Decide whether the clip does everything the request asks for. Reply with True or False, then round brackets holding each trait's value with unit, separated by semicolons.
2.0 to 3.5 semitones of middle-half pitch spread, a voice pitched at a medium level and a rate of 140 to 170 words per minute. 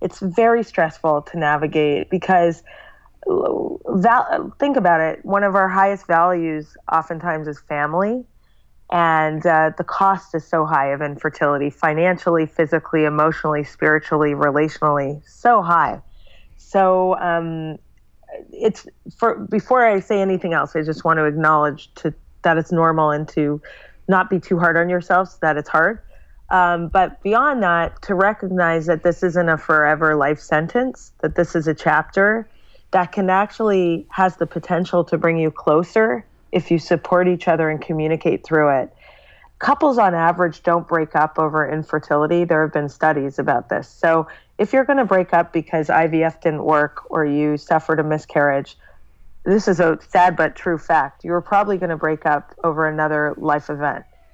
True (3.1 semitones; 165 Hz; 160 wpm)